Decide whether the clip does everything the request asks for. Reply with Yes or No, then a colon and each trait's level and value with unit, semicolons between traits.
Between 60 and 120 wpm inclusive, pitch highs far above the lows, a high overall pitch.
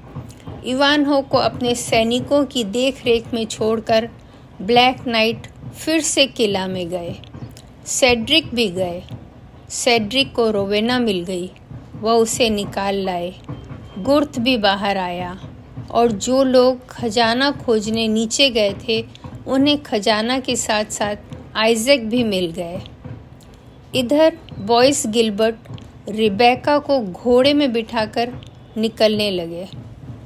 Yes: average, 115 wpm; wide, 5.7 semitones; high, 225 Hz